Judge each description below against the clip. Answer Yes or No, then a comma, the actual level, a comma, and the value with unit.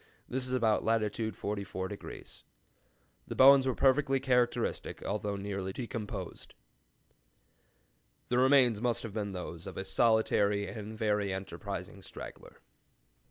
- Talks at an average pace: No, slow, 115 wpm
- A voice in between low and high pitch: No, low, 110 Hz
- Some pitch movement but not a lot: Yes, average, 3.6 semitones